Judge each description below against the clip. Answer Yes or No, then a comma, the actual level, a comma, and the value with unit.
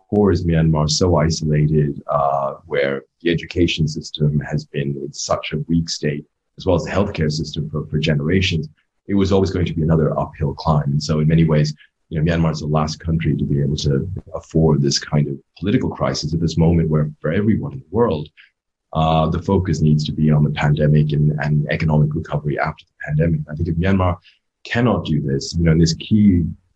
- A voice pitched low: Yes, very low, 80 Hz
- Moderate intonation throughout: No, narrow, 1.9 semitones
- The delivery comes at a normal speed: No, fast, 210 wpm